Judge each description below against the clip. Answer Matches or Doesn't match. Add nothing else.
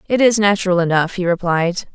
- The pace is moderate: Matches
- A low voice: Doesn't match